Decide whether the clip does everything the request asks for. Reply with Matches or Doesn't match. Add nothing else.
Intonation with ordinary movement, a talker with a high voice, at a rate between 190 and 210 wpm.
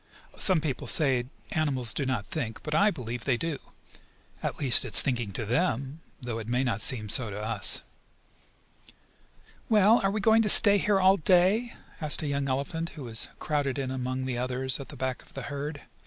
Doesn't match